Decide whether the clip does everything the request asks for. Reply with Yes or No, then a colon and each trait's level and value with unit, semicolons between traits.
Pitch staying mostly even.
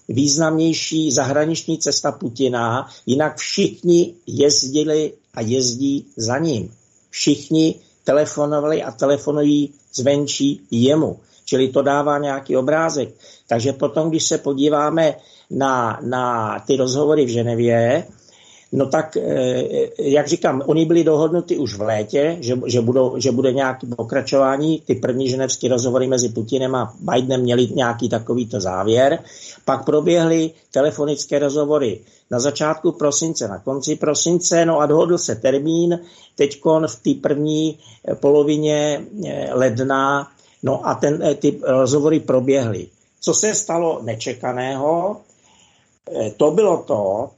No: average, 3.3 semitones